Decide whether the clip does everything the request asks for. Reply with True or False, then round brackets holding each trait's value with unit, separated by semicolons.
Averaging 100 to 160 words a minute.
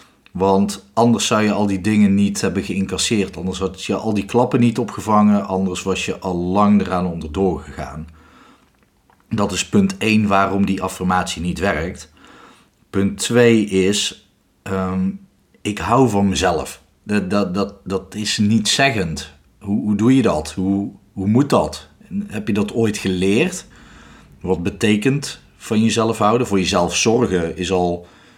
True (155 wpm)